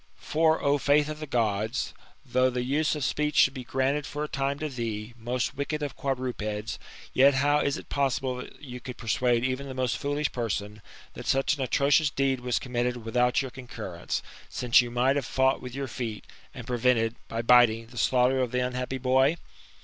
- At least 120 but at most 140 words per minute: No, average, 195 wpm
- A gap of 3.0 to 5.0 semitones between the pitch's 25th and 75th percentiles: No, narrow, 2.4 semitones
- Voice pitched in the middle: No, low, 130 Hz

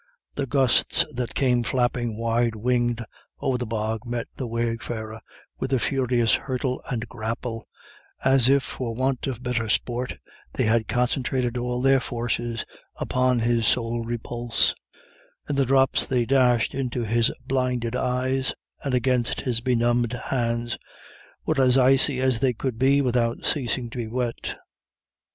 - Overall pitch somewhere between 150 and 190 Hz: No, low, 125 Hz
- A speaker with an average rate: Yes, average, 145 wpm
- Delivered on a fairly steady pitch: Yes, narrow, 1.8 semitones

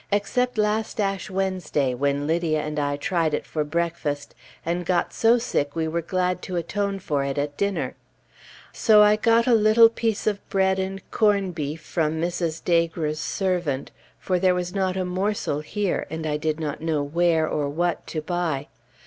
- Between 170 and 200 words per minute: Yes, average, 180 wpm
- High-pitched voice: No, medium, 175 Hz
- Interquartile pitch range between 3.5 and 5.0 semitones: Yes, average, 4.2 semitones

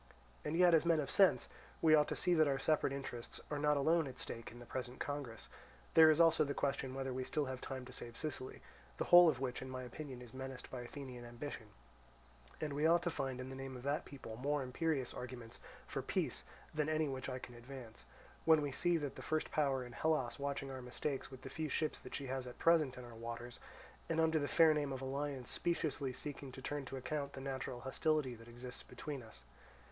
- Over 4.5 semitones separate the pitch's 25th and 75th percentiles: No, average, 3.1 semitones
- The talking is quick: Yes, fast, 225 wpm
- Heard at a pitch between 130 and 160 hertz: Yes, low, 135 Hz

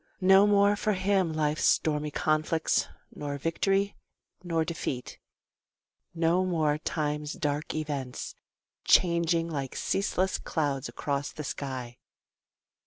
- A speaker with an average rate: No, slow, 105 wpm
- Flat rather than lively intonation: No, average, 3.8 semitones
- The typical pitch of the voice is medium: Yes, medium, 160 Hz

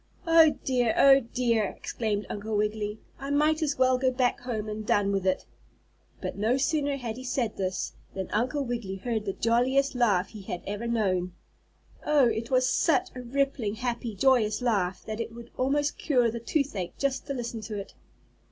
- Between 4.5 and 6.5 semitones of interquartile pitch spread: No, average, 4.0 semitones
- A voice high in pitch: Yes, high, 235 Hz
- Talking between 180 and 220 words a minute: Yes, average, 185 wpm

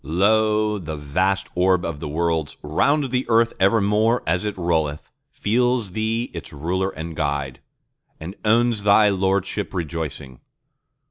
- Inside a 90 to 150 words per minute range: Yes, slow, 135 wpm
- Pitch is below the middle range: Yes, very low, 95 Hz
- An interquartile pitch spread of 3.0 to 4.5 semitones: No, average, 5.1 semitones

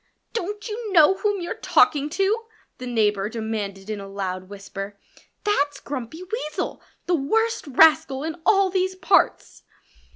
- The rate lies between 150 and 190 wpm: No, average, 140 wpm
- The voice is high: Yes, very high, 300 Hz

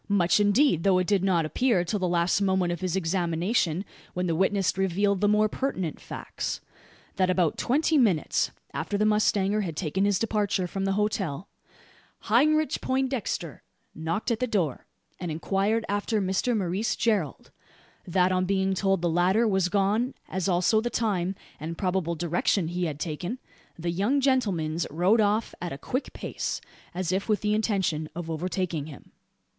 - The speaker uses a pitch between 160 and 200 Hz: Yes, high, 190 Hz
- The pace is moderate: Yes, average, 170 wpm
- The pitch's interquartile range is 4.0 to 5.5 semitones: No, average, 3.4 semitones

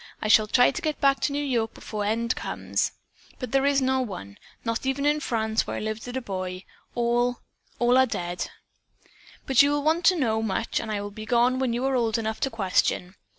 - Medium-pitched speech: No, high, 240 Hz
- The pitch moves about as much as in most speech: Yes, average, 3.6 semitones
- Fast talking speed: Yes, fast, 230 wpm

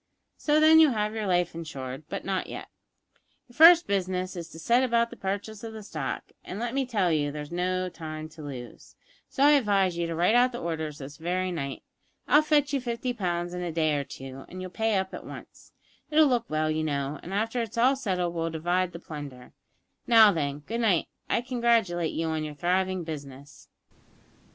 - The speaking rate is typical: No, fast, 210 wpm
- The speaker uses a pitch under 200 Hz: Yes, medium, 185 Hz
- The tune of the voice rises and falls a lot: Yes, wide, 6.7 semitones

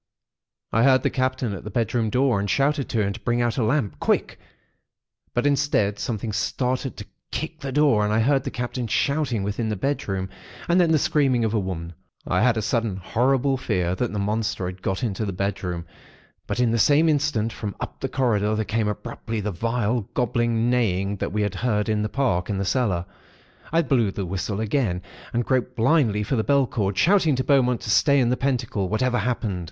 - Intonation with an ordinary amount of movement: Yes, average, 4.1 semitones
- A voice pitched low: Yes, low, 115 Hz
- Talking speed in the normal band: No, fast, 210 wpm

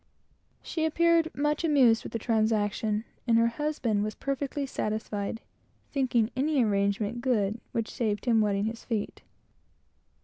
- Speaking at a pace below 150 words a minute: Yes, slow, 135 wpm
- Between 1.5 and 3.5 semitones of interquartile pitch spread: No, average, 4.5 semitones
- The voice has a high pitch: Yes, high, 230 Hz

